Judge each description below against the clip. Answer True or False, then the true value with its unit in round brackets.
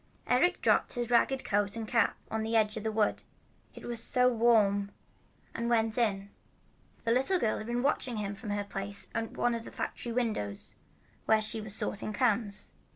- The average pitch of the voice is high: True (225 Hz)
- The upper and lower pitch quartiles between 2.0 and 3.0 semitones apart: True (2.5 semitones)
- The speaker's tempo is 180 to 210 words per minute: True (190 wpm)